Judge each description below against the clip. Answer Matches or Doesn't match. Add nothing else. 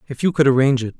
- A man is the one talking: Matches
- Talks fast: Matches